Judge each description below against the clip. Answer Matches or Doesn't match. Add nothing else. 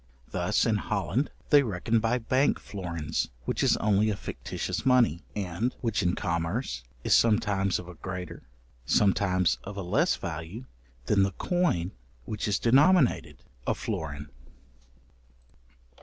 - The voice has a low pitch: Matches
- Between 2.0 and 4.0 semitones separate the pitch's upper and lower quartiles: Doesn't match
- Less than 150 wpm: Matches